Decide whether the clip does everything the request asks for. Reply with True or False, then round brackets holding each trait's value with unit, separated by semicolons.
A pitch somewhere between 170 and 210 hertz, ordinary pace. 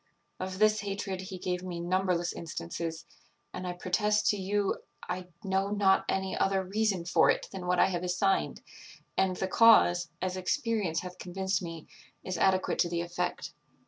True (185 Hz; 170 wpm)